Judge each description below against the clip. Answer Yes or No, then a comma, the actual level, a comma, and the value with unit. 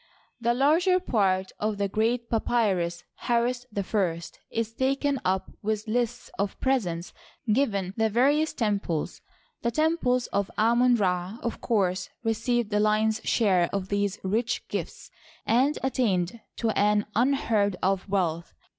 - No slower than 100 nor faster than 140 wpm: Yes, slow, 135 wpm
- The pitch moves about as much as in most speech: Yes, average, 3.7 semitones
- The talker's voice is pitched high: Yes, high, 220 Hz